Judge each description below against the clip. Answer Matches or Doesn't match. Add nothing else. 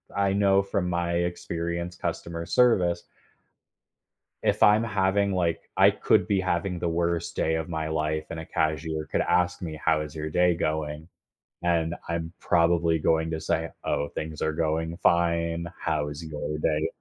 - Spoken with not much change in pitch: Matches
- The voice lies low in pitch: Matches